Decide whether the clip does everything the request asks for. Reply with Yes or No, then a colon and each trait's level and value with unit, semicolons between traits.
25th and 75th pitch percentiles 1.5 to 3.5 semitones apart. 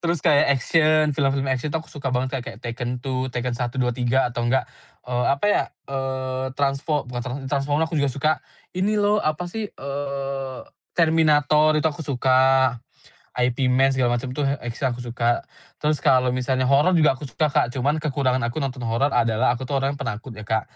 Yes: average, 2.7 semitones